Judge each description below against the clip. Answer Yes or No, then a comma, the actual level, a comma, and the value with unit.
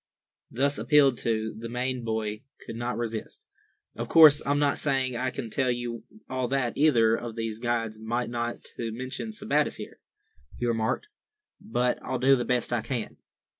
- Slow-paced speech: No, average, 170 wpm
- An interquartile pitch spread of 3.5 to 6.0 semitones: No, narrow, 2.6 semitones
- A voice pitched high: No, low, 120 Hz